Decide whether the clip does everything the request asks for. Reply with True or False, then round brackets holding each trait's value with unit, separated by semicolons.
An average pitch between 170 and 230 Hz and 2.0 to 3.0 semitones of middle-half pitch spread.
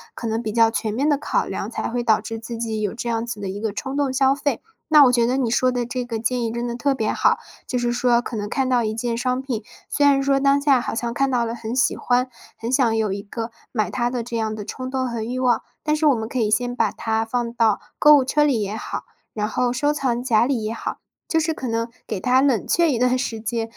False (240 Hz; 2.5 semitones)